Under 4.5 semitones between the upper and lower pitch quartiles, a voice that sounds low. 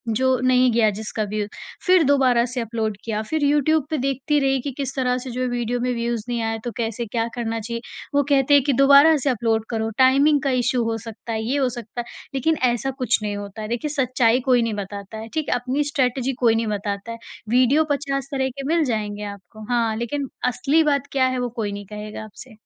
No: average, 3.5 semitones; high, 245 Hz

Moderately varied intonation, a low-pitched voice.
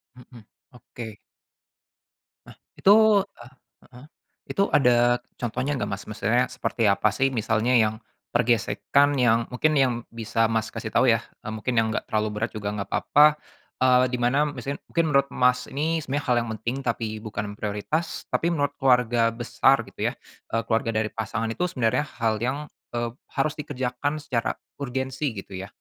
Yes: average, 3.2 semitones; low, 120 Hz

